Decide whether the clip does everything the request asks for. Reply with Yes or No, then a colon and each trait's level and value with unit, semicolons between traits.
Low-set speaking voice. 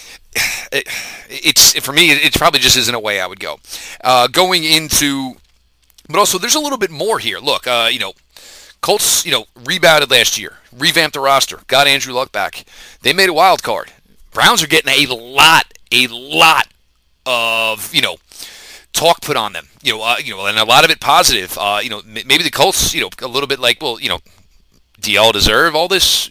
Yes: low, 130 Hz